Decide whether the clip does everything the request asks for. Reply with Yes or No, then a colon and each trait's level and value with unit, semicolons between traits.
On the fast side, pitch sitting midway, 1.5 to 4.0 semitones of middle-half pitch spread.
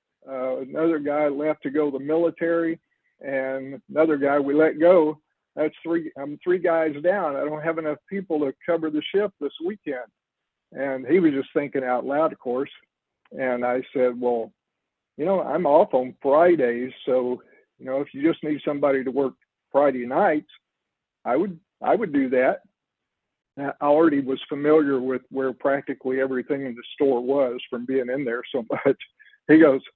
No: average, 180 wpm; medium, 145 Hz; average, 3.2 semitones